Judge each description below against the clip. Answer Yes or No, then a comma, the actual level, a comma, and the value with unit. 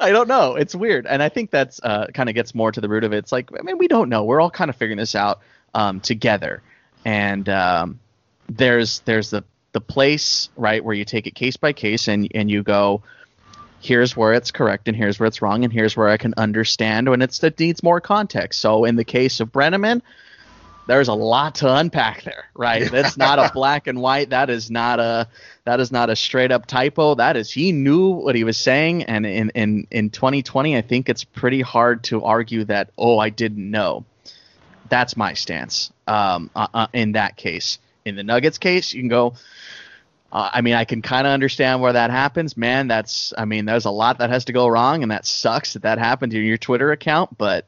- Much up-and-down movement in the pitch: No, average, 3.6 semitones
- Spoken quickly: Yes, fast, 225 wpm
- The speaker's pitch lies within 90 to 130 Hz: Yes, low, 120 Hz